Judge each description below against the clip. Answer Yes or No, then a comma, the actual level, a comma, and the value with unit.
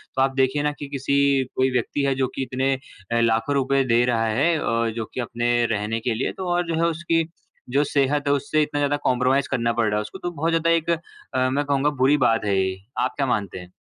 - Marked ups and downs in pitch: No, average, 3.7 semitones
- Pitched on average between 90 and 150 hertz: Yes, low, 135 Hz